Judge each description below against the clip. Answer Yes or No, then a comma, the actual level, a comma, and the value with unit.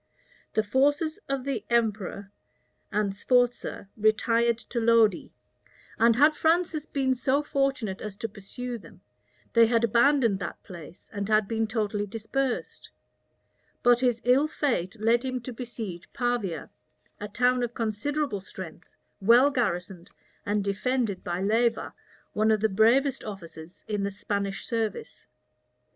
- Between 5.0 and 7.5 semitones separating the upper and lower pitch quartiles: No, average, 3.8 semitones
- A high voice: Yes, high, 225 Hz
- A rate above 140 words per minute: No, slow, 135 wpm